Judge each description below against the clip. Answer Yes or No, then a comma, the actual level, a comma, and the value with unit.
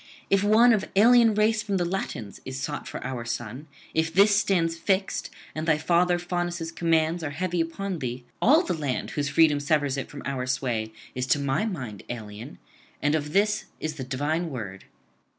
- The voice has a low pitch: No, medium, 160 Hz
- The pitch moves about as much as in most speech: No, wide, 5.7 semitones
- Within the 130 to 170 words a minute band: No, average, 185 wpm